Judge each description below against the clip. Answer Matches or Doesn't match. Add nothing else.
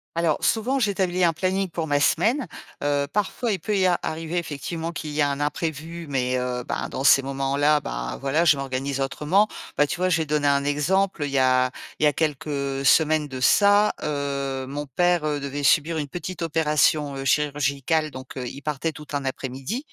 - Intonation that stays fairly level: Doesn't match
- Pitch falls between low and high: Matches